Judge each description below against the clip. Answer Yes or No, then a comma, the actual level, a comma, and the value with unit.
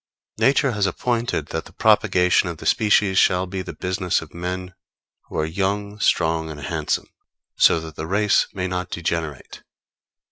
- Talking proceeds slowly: No, average, 165 wpm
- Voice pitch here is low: Yes, very low, 90 Hz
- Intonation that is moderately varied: Yes, average, 3.7 semitones